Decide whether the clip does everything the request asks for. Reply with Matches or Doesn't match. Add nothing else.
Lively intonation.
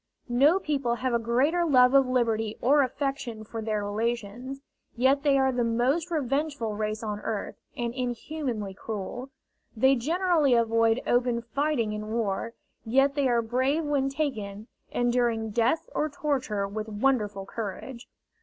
Doesn't match